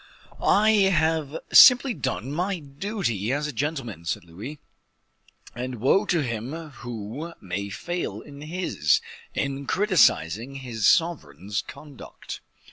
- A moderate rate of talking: No, slow, 120 wpm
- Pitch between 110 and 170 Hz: Yes, medium, 140 Hz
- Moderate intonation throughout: No, wide, 6.6 semitones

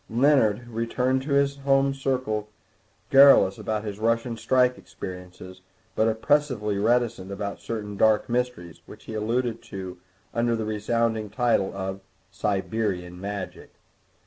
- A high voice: No, low, 110 Hz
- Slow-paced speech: Yes, slow, 125 wpm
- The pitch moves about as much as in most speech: Yes, average, 3.6 semitones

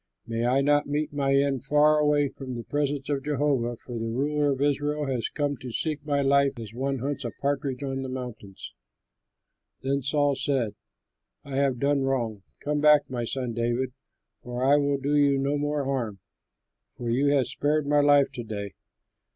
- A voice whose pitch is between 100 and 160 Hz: Yes, medium, 140 Hz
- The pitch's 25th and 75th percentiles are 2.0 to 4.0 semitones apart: Yes, narrow, 2.6 semitones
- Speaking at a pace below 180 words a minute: No, average, 190 wpm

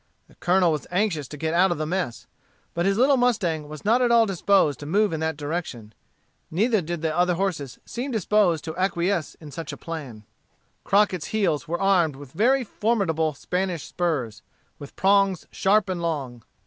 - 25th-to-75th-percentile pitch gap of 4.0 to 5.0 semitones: Yes, average, 4.5 semitones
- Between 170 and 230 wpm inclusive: Yes, average, 185 wpm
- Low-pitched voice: No, medium, 175 Hz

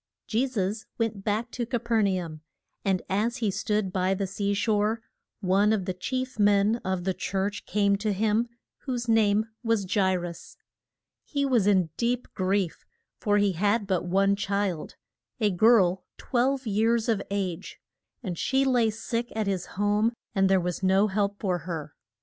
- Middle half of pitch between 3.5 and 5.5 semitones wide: No, average, 3.0 semitones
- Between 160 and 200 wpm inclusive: Yes, average, 175 wpm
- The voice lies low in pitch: No, high, 205 Hz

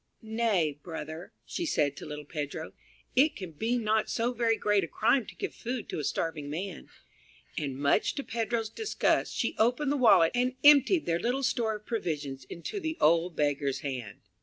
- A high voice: Yes, high, 205 Hz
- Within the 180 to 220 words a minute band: Yes, average, 185 wpm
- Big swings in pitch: Yes, wide, 8.3 semitones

